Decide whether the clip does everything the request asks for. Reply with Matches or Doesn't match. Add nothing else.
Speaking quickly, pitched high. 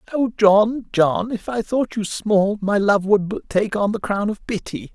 Matches